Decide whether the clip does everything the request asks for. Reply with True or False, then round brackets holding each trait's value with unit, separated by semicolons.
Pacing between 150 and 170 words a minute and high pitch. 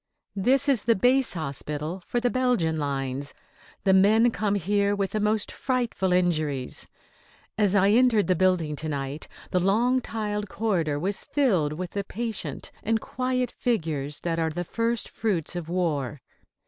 True (160 wpm; 195 Hz)